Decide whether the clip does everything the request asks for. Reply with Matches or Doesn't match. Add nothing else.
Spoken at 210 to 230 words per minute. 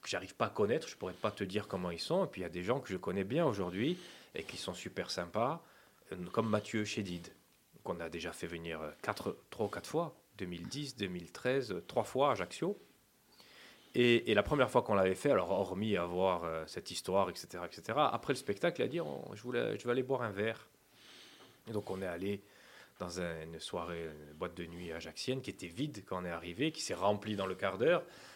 Matches